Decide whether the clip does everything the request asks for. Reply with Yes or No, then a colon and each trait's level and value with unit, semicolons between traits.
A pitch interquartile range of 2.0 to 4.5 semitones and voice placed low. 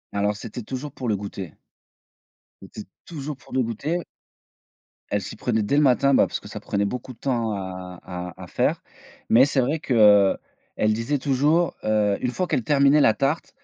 No: average, 5.2 semitones; low, 120 Hz